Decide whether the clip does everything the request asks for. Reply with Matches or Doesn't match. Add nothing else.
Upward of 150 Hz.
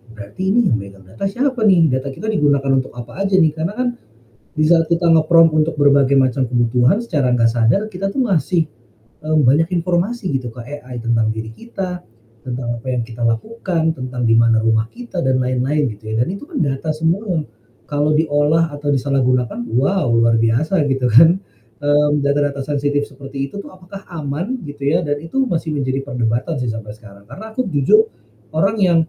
Doesn't match